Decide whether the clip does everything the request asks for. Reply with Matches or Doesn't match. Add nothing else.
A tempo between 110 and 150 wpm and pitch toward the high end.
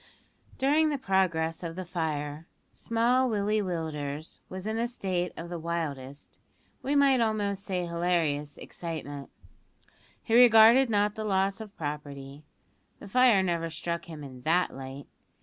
Doesn't match